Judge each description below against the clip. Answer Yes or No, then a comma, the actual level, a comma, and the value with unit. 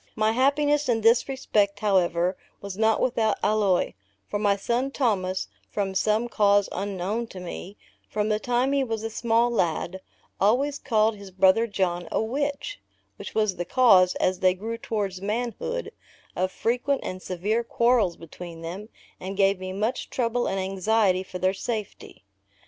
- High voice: Yes, high, 210 Hz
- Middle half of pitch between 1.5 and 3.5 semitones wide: No, average, 3.9 semitones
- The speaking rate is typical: Yes, average, 160 wpm